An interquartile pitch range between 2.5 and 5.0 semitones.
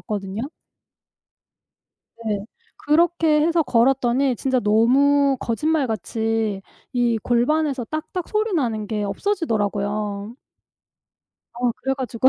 No: wide, 5.6 semitones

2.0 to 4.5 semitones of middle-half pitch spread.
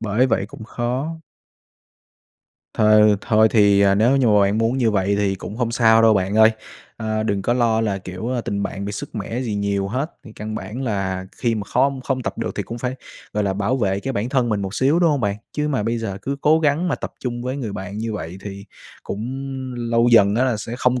Yes: average, 3.8 semitones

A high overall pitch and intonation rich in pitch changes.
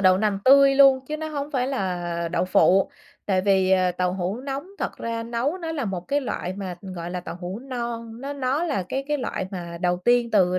Yes: high, 220 Hz; wide, 6.8 semitones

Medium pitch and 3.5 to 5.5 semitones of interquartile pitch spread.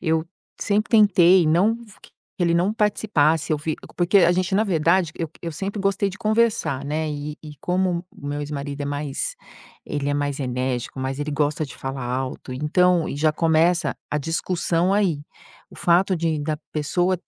Yes: medium, 160 Hz; average, 4.1 semitones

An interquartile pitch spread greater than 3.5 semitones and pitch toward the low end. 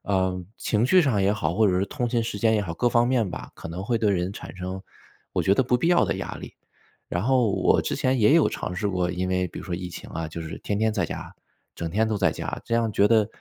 Yes: average, 4.2 semitones; low, 100 Hz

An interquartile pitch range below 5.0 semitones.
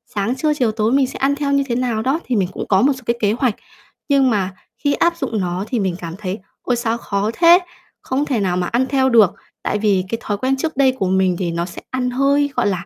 No: average, 5.3 semitones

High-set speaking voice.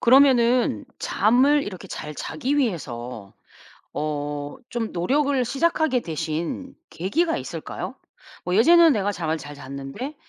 Yes: high, 225 Hz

